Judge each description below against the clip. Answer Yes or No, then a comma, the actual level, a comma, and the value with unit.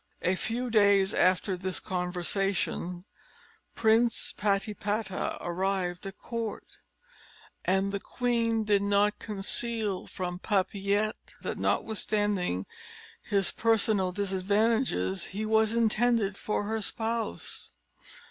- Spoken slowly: Yes, slow, 100 wpm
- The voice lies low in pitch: No, high, 205 Hz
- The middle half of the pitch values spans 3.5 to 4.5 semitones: No, narrow, 2.6 semitones